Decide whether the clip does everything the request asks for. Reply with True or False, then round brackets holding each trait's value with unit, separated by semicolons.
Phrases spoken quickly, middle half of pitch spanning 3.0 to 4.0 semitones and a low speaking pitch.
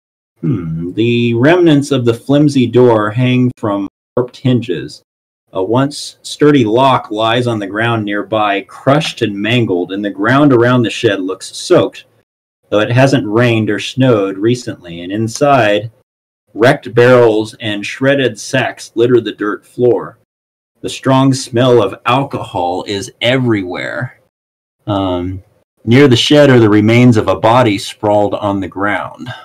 False (145 wpm; 3.7 semitones; 115 Hz)